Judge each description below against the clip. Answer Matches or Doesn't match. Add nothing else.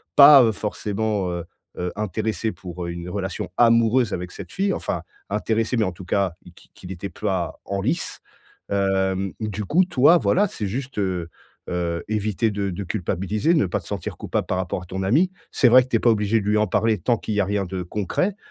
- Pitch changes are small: Doesn't match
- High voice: Doesn't match